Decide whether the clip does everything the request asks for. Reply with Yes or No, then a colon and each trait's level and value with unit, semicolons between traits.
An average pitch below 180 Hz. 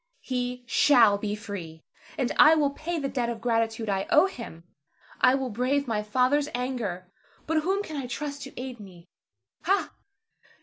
No: very high, 250 Hz